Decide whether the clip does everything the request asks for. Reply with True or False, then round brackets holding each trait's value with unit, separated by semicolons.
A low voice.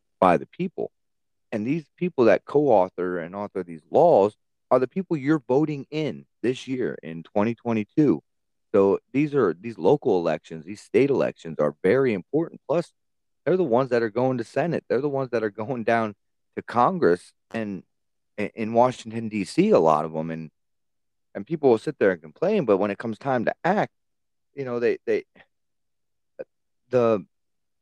True (115 Hz)